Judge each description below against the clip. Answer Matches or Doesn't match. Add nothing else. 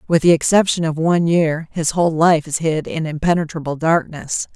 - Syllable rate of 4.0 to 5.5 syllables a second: Matches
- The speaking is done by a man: Doesn't match